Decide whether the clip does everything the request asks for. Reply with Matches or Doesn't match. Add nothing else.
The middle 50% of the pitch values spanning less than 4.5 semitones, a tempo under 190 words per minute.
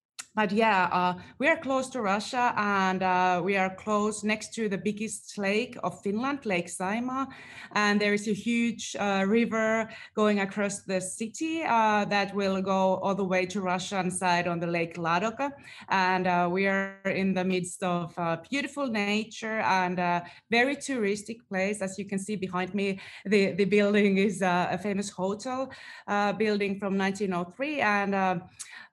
Matches